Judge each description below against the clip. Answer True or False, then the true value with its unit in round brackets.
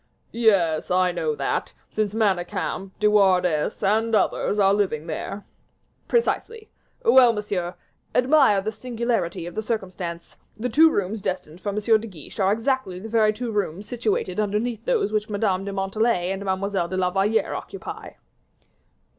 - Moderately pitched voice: False (205 Hz)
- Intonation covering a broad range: False (3.3 semitones)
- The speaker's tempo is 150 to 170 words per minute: True (155 wpm)